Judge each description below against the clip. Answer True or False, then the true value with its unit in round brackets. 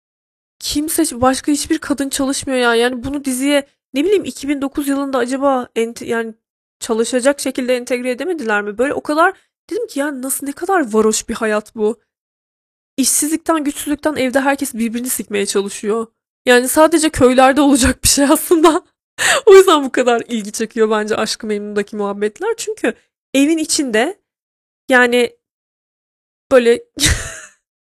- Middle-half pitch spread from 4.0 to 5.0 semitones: True (4.4 semitones)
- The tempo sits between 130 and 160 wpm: True (140 wpm)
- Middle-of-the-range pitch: False (265 Hz)